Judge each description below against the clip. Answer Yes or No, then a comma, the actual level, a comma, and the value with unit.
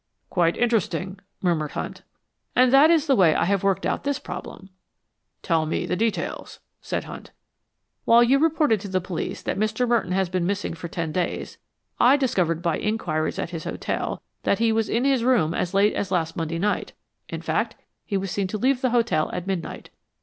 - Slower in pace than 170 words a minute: No, average, 195 wpm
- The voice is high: Yes, high, 195 Hz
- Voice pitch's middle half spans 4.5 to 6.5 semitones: Yes, wide, 5.5 semitones